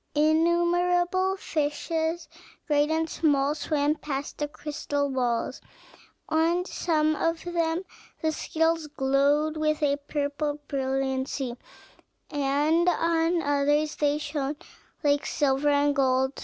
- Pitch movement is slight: Yes, narrow, 2.3 semitones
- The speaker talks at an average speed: No, slow, 110 wpm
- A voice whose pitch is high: Yes, very high, 300 Hz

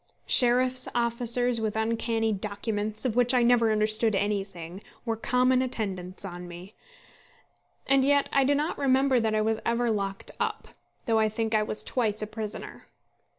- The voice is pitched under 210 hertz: No, high, 225 Hz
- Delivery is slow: No, average, 160 wpm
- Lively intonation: No, average, 2.7 semitones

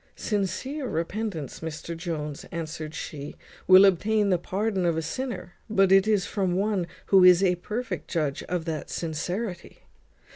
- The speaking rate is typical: Yes, average, 150 wpm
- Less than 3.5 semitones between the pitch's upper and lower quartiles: No, average, 3.8 semitones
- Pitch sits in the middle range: Yes, medium, 180 Hz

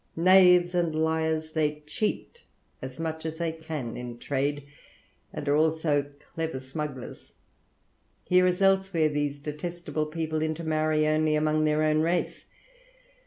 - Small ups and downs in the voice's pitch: Yes, narrow, 1.6 semitones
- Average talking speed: No, slow, 130 wpm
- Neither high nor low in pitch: Yes, medium, 155 Hz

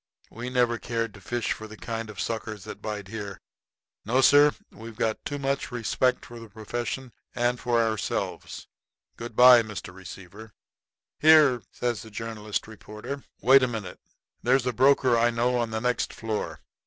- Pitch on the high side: No, low, 115 Hz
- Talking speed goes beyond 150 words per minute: Yes, average, 175 wpm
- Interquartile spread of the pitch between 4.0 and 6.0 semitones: No, narrow, 2.4 semitones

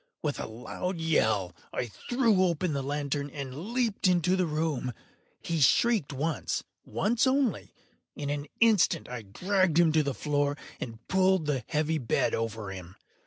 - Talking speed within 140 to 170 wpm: Yes, average, 155 wpm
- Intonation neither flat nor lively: No, wide, 5.7 semitones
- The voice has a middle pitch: Yes, medium, 155 Hz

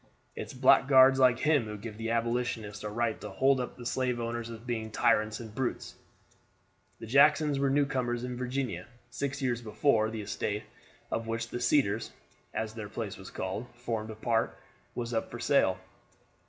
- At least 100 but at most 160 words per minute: No, average, 180 wpm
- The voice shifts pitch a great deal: No, average, 2.7 semitones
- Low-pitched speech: Yes, low, 120 Hz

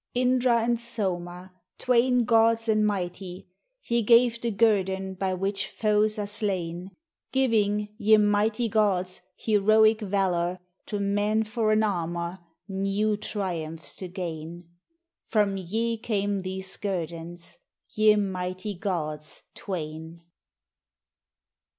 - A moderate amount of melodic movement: Yes, average, 3.2 semitones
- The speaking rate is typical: No, slow, 115 wpm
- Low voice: No, high, 200 Hz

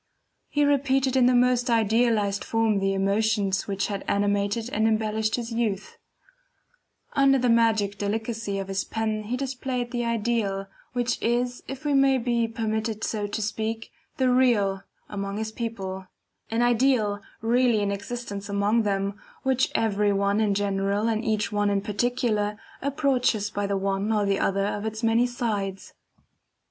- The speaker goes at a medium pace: Yes, average, 155 wpm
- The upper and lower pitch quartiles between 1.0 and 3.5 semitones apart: Yes, average, 3.1 semitones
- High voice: Yes, high, 220 Hz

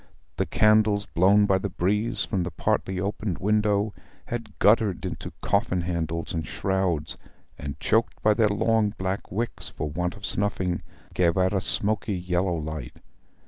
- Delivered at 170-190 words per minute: No, average, 155 wpm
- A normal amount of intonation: Yes, average, 3.0 semitones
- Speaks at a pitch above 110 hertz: No, very low, 95 Hz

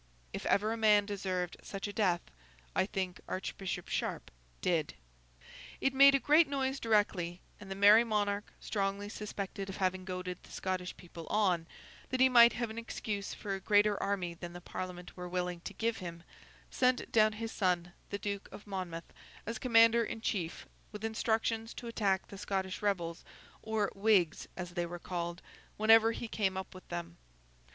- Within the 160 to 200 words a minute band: Yes, average, 170 wpm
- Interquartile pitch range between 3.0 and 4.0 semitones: Yes, average, 3.4 semitones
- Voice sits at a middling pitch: No, high, 200 Hz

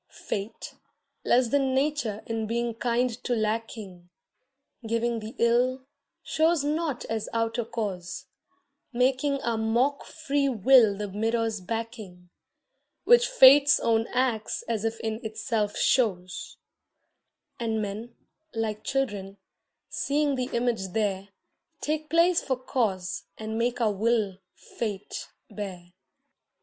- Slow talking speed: Yes, slow, 115 wpm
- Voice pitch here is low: No, high, 230 Hz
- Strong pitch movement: No, average, 3.4 semitones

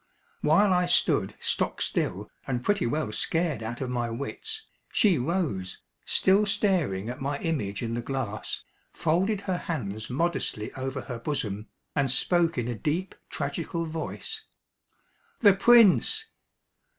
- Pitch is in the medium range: Yes, medium, 150 Hz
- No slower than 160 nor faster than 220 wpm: No, average, 140 wpm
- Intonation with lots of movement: Yes, wide, 7.5 semitones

